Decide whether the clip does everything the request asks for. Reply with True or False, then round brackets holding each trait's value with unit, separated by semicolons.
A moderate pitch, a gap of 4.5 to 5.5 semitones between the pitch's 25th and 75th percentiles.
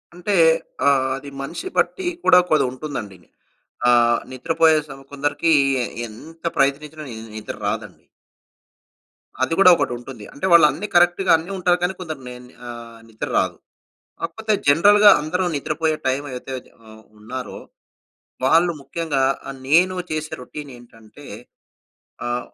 True (145 Hz; 4.9 semitones)